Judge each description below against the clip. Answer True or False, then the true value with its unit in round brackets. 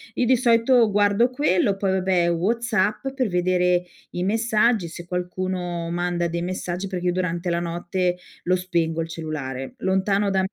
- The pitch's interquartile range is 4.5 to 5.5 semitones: False (2.8 semitones)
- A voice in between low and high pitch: True (180 Hz)